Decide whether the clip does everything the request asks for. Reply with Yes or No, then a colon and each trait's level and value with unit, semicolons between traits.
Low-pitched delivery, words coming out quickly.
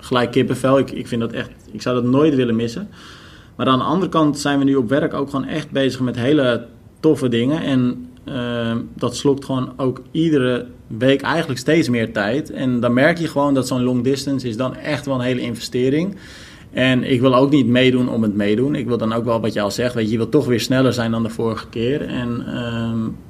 Yes: low, 125 Hz; fast, 235 wpm